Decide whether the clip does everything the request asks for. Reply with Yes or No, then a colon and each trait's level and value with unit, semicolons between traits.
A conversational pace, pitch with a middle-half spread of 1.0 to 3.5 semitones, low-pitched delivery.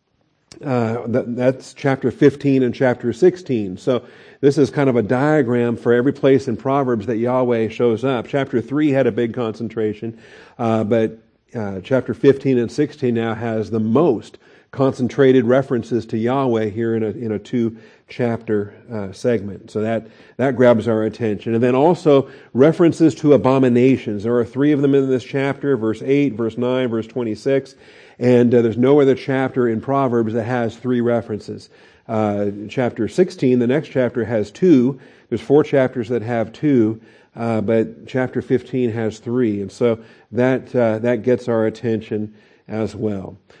Yes: average, 165 wpm; average, 2.9 semitones; low, 120 Hz